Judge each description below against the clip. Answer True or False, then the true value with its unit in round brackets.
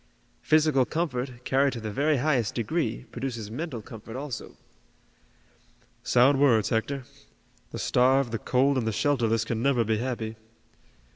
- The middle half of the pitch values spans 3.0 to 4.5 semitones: True (3.4 semitones)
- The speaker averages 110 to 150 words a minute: True (140 wpm)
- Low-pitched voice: True (125 Hz)